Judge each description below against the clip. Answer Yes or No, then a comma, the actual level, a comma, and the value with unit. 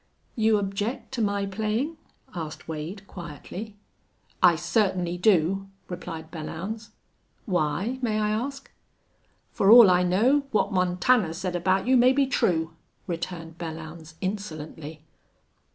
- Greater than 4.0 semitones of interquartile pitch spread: Yes, average, 4.4 semitones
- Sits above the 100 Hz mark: Yes, high, 190 Hz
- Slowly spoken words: Yes, slow, 120 wpm